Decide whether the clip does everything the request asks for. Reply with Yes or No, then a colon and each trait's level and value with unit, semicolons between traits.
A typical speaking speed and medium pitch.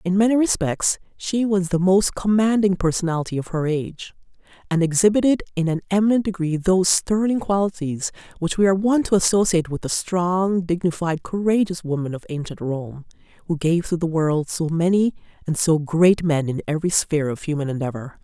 Yes: average, 175 wpm; medium, 175 Hz